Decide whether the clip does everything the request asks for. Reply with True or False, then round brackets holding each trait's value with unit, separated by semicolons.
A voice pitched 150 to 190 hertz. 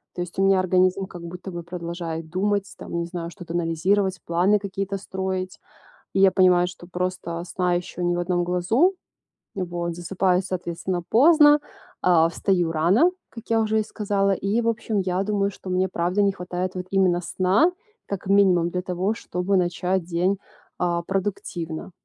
True (185 Hz)